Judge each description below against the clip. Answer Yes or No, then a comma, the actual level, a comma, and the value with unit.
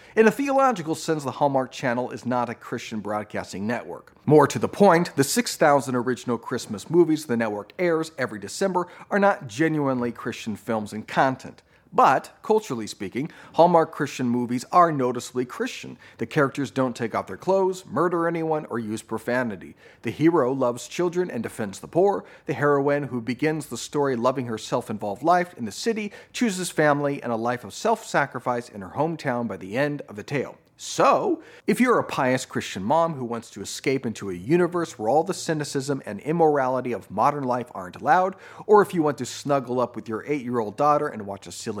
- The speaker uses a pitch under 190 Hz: Yes, low, 135 Hz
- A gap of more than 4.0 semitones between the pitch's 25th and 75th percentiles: Yes, wide, 5.6 semitones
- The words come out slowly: No, average, 195 wpm